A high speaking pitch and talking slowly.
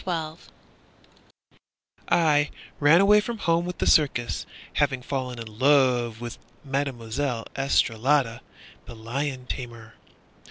No: low, 135 Hz; slow, 115 wpm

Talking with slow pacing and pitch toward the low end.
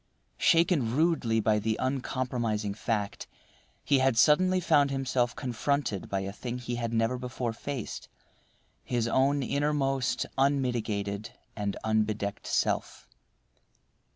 Yes: slow, 110 wpm; low, 125 Hz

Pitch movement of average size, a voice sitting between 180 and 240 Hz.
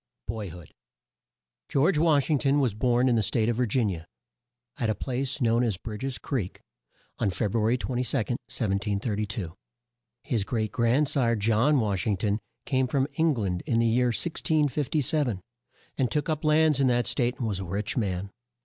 No: average, 4.4 semitones; low, 120 Hz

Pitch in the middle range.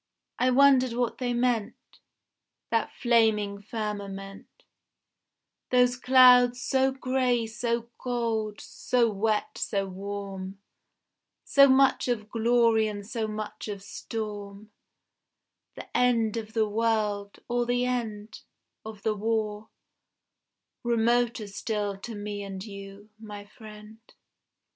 No: high, 220 Hz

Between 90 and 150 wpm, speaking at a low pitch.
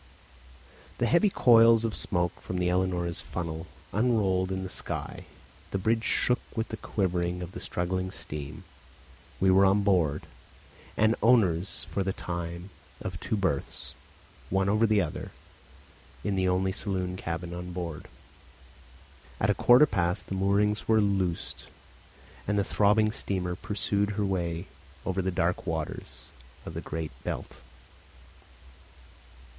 Yes: average, 140 wpm; very low, 95 Hz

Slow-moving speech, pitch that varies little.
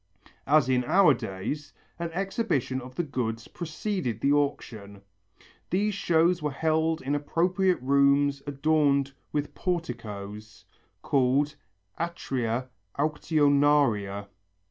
No: slow, 100 wpm; average, 4.4 semitones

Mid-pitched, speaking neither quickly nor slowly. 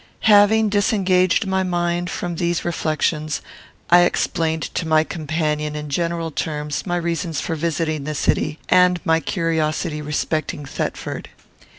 No: medium, 165 Hz; slow, 130 wpm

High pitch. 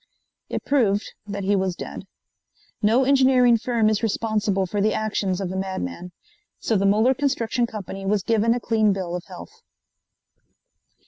Yes: high, 210 Hz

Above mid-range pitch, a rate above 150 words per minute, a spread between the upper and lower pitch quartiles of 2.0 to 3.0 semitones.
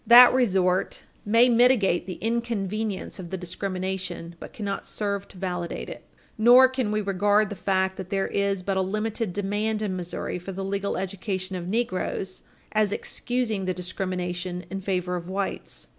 Yes: high, 195 Hz; average, 165 wpm; narrow, 2.5 semitones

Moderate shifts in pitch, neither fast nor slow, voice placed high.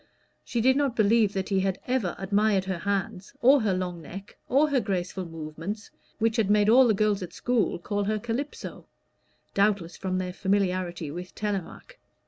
Yes: average, 3.3 semitones; average, 175 wpm; high, 200 Hz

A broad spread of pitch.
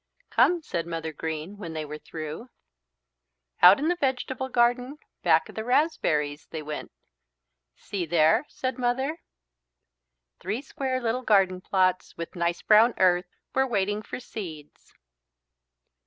Yes: wide, 7.4 semitones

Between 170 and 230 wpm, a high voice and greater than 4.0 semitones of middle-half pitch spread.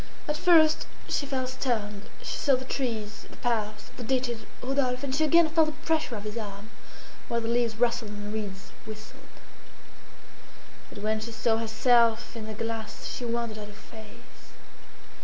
No: average, 175 wpm; high, 230 Hz; average, 3.3 semitones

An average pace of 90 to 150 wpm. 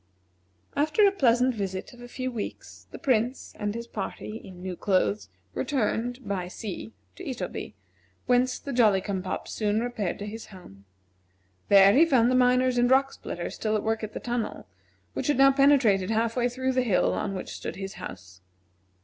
No: average, 185 wpm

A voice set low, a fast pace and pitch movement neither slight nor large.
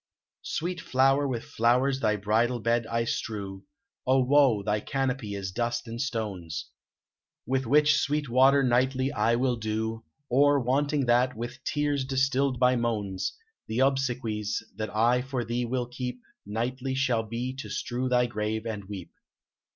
No: low, 125 Hz; average, 150 wpm; average, 3.0 semitones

